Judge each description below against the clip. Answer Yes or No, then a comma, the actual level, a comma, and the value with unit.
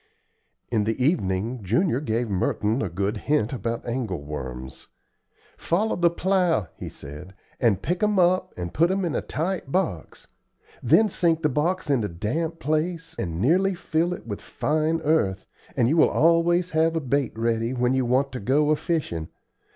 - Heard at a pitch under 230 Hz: Yes, medium, 140 Hz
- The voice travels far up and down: Yes, wide, 7.8 semitones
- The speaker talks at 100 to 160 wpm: No, average, 170 wpm